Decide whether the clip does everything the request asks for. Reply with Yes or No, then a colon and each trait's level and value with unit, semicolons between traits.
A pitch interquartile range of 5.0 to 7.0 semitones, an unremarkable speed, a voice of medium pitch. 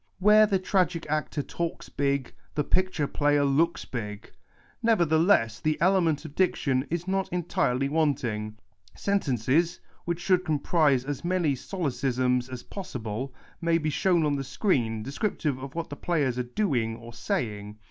Yes: wide, 5.4 semitones; average, 150 wpm; medium, 145 Hz